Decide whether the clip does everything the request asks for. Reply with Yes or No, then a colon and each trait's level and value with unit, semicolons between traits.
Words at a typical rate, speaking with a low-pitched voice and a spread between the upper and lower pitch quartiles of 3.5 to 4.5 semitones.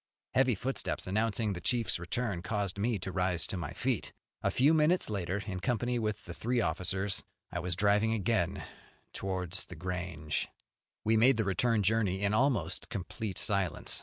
Yes: average, 165 wpm; low, 100 Hz; average, 3.9 semitones